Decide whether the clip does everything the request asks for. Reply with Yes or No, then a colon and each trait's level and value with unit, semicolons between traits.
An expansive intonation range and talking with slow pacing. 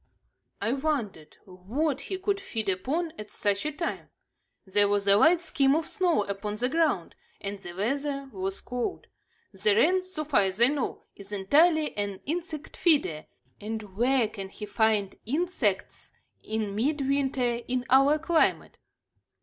No: wide, 7.1 semitones; average, 150 wpm